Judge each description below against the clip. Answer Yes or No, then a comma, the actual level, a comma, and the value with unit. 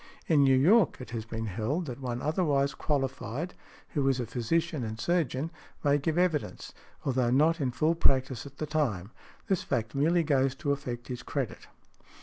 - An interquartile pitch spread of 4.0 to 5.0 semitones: Yes, average, 4.3 semitones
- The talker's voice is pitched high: No, medium, 140 Hz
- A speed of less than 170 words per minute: No, average, 180 wpm